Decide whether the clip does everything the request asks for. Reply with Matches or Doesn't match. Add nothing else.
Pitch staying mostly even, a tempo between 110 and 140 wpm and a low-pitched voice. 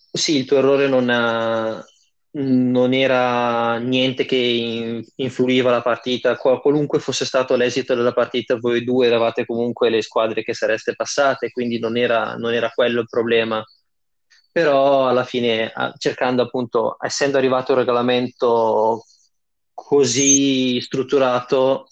Matches